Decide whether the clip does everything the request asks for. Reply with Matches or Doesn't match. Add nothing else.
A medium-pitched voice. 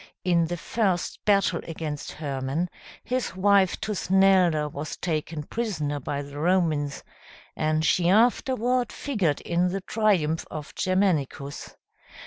Matches